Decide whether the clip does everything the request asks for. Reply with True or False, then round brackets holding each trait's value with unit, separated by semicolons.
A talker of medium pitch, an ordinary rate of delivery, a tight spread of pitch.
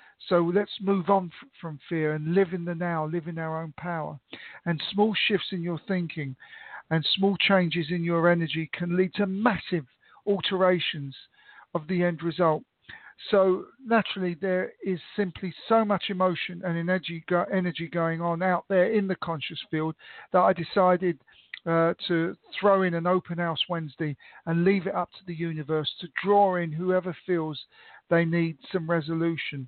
True (175 Hz; 165 wpm; 2.2 semitones)